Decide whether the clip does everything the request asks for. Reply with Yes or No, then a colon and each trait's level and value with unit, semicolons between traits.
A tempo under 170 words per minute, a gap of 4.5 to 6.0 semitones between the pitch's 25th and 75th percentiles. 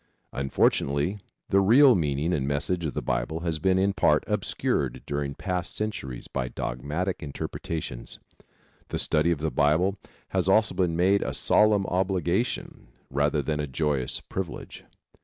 Yes: average, 145 wpm; average, 4.9 semitones